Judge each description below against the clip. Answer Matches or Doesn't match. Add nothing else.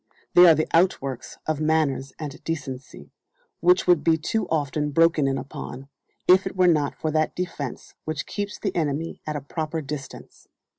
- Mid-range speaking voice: Matches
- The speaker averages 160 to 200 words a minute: Matches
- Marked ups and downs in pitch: Doesn't match